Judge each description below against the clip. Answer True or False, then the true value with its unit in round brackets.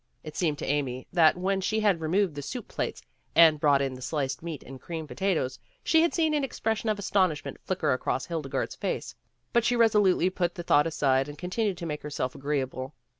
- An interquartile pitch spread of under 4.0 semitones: False (5.4 semitones)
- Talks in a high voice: False (165 Hz)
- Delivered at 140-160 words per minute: False (205 wpm)